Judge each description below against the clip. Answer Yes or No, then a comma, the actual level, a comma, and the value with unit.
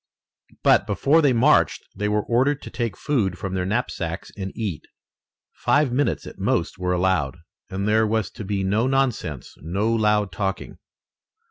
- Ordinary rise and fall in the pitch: Yes, average, 4.2 semitones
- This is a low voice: Yes, low, 105 Hz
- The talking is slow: No, average, 160 wpm